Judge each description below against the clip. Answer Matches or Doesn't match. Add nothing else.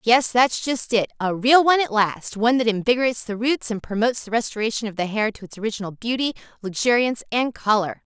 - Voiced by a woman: Matches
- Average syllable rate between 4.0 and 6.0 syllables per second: Doesn't match